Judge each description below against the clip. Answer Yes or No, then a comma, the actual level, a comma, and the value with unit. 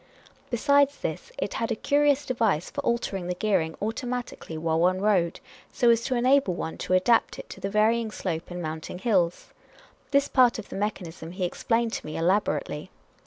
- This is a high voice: Yes, high, 210 Hz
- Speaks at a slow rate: No, average, 185 wpm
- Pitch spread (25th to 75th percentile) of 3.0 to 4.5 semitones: No, average, 5.2 semitones